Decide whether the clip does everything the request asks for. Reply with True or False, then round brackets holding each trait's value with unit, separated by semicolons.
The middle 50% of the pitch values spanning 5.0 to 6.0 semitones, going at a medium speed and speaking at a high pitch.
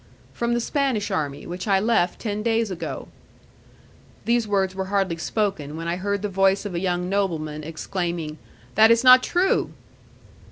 False (4.0 semitones; 165 wpm; 195 Hz)